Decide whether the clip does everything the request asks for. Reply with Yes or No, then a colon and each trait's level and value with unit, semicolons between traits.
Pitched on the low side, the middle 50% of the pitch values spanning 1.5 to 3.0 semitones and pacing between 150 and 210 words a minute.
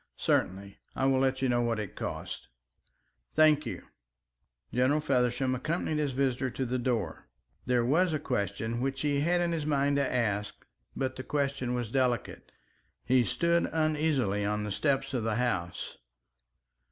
No: low, 130 Hz; average, 3.4 semitones; average, 165 wpm